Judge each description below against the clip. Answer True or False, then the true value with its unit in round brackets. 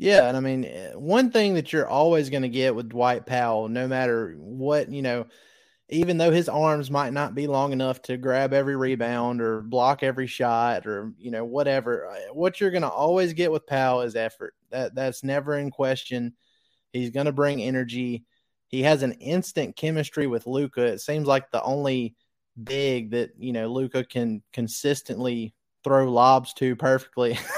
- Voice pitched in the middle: False (130 Hz)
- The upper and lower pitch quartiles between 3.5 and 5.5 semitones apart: False (3.0 semitones)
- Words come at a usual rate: True (175 wpm)